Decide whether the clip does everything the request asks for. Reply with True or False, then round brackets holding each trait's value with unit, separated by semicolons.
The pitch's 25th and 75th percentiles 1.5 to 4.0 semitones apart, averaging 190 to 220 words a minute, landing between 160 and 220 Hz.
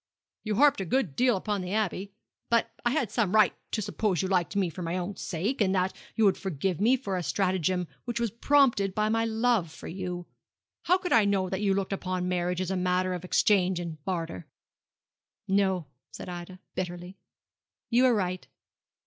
True (3.1 semitones; 195 wpm; 190 Hz)